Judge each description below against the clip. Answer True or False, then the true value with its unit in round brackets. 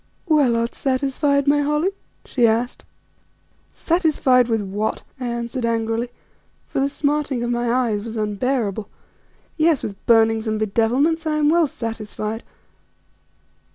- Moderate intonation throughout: True (4.2 semitones)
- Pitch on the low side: False (240 Hz)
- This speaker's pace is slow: True (130 wpm)